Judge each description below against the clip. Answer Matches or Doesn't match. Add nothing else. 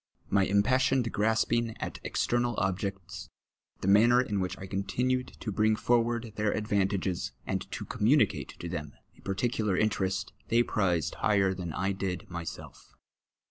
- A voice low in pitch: Matches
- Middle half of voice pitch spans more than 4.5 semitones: Doesn't match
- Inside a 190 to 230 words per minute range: Doesn't match